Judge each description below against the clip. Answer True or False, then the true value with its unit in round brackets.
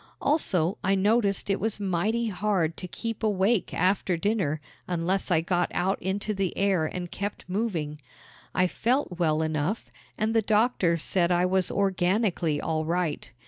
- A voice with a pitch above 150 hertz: True (190 Hz)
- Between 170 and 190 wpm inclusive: False (155 wpm)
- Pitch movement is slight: False (3.5 semitones)